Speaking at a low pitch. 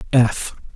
Yes: low, 120 Hz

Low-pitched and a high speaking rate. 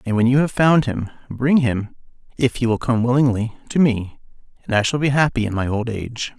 Yes: low, 120 Hz; fast, 225 wpm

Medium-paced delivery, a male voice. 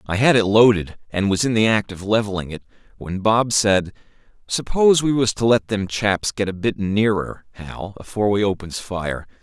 Yes: average, 195 wpm; male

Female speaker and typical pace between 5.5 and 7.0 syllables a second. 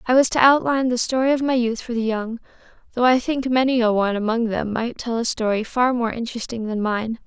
Yes: female; 6.0 syllables/s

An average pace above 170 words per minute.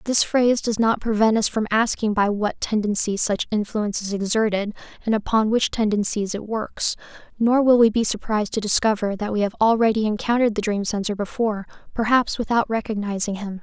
Yes: average, 180 wpm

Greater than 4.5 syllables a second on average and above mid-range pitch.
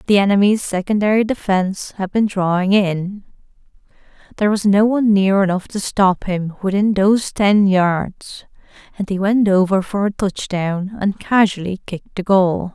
Yes: 4.8 syllables/s; high, 195 Hz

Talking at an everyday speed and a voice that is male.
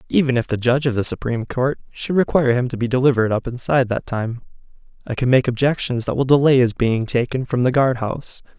No: fast, 225 wpm; male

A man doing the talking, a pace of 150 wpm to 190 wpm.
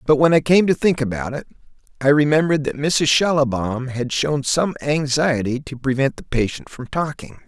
Yes: male; average, 185 wpm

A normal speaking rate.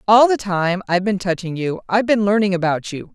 No: fast, 230 wpm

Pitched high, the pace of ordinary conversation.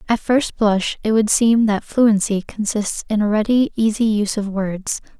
Yes: high, 215 Hz; average, 185 wpm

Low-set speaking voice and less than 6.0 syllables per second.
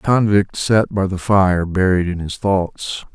Yes: very low, 95 Hz; 4.0 syllables/s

